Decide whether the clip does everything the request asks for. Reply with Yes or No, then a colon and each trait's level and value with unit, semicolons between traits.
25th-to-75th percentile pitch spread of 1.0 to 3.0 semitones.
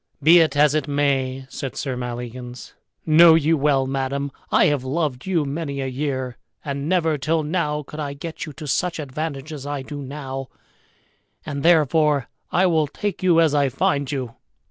Yes: average, 2.7 semitones